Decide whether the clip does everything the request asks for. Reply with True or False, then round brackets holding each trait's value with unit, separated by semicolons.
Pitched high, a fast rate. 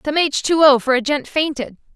True (280 Hz; 245 wpm)